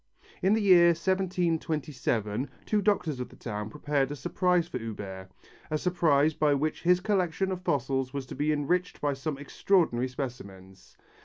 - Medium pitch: Yes, medium, 150 Hz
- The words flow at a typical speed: Yes, average, 160 wpm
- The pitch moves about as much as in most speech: No, wide, 5.7 semitones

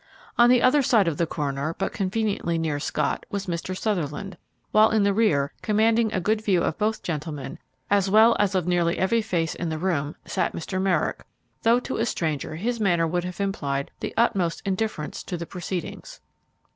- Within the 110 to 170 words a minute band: No, average, 190 wpm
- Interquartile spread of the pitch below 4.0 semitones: No, average, 4.7 semitones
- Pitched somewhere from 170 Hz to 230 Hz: Yes, medium, 185 Hz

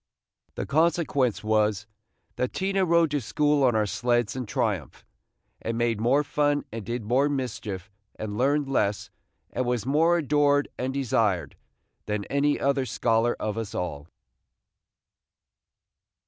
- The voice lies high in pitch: No, low, 125 Hz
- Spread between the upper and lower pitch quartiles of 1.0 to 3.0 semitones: No, average, 5.0 semitones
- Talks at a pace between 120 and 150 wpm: Yes, slow, 135 wpm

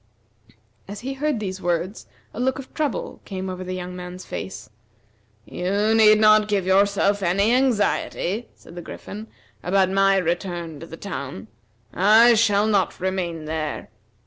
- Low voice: No, high, 195 Hz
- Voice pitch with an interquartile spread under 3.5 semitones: Yes, average, 3.1 semitones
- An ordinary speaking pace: Yes, average, 150 wpm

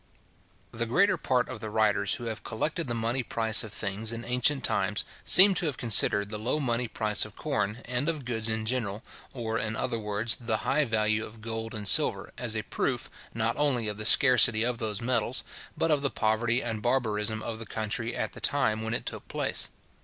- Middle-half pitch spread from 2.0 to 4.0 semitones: Yes, narrow, 2.4 semitones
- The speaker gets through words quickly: Yes, fast, 210 wpm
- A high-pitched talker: No, low, 115 Hz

